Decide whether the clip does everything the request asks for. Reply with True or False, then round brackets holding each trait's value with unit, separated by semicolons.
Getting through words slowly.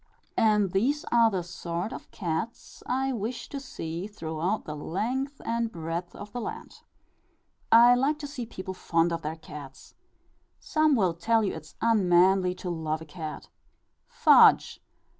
False (160 wpm)